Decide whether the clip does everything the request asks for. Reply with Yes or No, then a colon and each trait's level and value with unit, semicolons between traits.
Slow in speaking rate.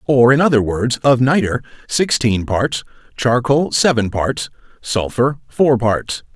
Yes: slow, 130 wpm